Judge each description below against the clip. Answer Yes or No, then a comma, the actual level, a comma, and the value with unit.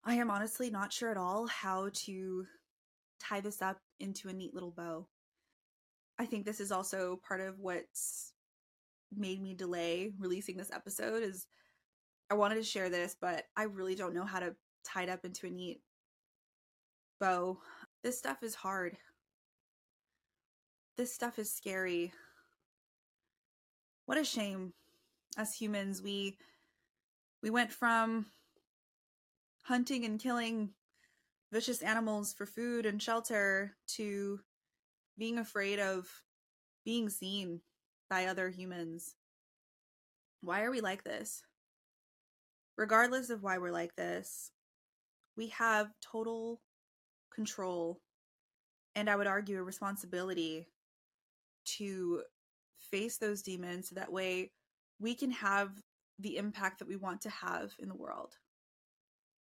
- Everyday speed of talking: No, slow, 130 wpm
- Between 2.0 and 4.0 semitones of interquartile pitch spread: Yes, average, 3.2 semitones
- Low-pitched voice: No, high, 200 Hz